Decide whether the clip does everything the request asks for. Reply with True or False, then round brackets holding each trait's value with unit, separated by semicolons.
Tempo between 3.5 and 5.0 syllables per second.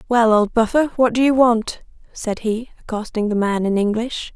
True (4.9 syllables/s)